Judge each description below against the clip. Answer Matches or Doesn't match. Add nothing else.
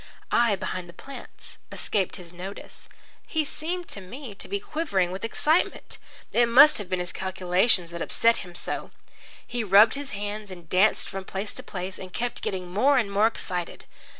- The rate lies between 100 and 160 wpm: Doesn't match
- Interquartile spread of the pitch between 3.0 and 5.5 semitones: Matches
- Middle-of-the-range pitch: Doesn't match